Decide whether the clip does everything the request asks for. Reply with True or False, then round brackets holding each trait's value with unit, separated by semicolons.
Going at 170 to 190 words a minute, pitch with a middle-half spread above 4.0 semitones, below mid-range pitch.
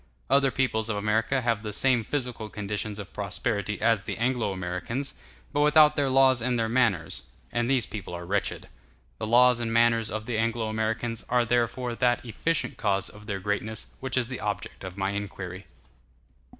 False (180 wpm; 3.1 semitones; 115 Hz)